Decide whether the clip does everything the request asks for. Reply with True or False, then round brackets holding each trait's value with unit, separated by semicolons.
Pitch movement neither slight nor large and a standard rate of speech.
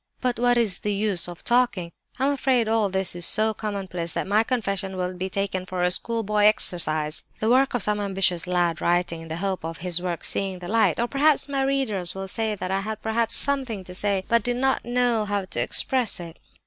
False (4.4 semitones; 215 wpm)